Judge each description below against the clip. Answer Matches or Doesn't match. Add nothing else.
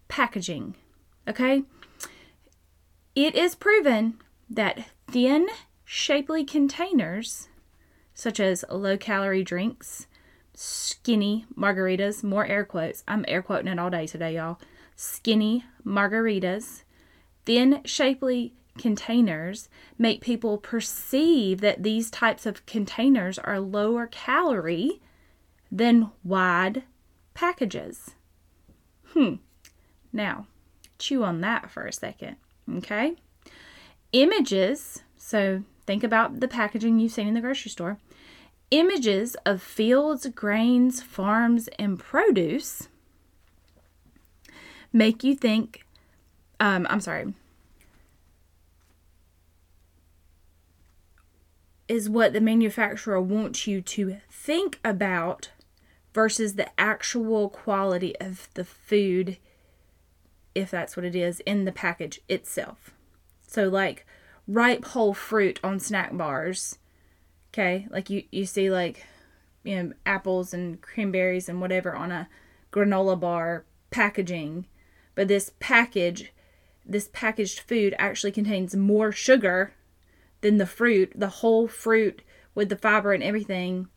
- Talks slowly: Matches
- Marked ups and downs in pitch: Doesn't match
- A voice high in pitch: Matches